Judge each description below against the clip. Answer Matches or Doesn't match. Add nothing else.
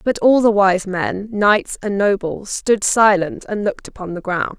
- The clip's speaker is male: Doesn't match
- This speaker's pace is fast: Doesn't match